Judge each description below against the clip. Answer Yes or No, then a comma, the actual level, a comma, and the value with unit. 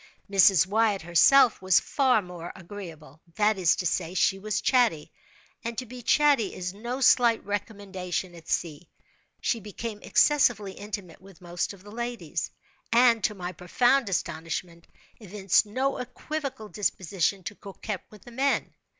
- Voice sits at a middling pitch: No, high, 205 Hz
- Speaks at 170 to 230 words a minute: No, average, 150 wpm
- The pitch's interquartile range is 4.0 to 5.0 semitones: Yes, average, 4.7 semitones